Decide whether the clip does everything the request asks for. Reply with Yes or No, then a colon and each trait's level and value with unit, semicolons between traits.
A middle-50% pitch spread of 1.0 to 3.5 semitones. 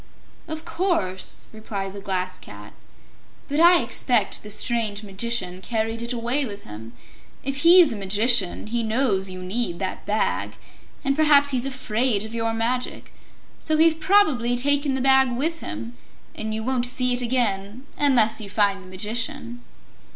No: average, 4.8 semitones